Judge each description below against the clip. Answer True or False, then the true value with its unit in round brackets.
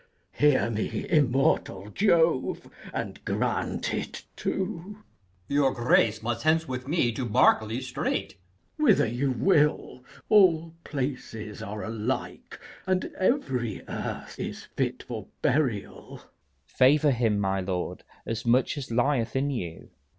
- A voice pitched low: True (130 Hz)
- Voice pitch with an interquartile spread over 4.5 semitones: True (5.1 semitones)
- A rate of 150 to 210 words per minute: False (135 wpm)